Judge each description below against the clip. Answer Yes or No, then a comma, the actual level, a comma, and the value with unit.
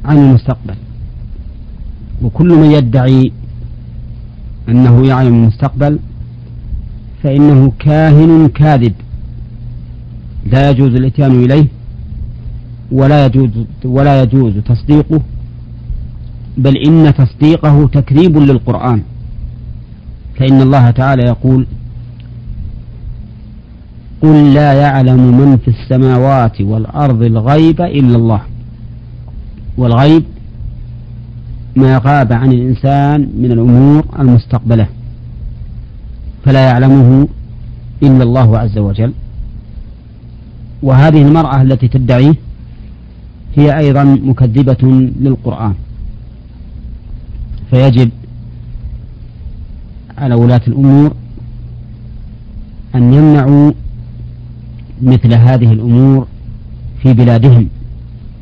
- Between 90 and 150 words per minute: No, average, 75 wpm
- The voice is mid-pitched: No, low, 125 Hz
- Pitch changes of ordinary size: Yes, average, 3.0 semitones